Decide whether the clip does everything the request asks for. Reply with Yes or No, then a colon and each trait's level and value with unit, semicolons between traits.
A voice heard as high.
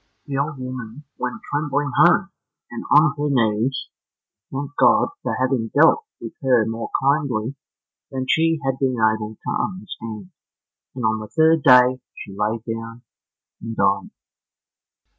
No: low, 130 Hz